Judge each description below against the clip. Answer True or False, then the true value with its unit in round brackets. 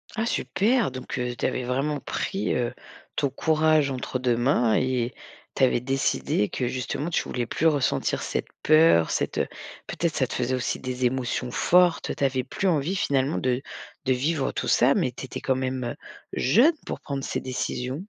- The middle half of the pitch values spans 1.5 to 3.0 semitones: False (3.6 semitones)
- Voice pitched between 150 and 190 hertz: False (130 Hz)